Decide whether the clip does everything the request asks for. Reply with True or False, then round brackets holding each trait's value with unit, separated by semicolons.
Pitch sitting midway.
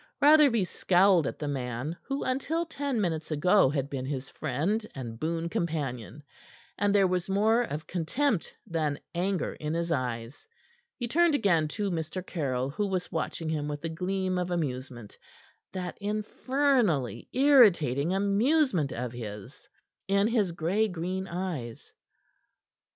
True (175 Hz)